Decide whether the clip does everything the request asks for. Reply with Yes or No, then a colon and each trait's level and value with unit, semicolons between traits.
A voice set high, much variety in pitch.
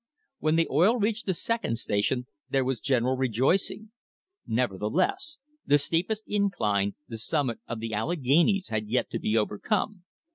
No: low, 135 Hz; wide, 8.9 semitones